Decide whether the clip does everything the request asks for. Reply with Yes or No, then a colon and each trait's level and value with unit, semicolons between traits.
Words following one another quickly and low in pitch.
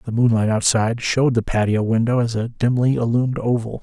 No: average, 190 wpm; low, 115 Hz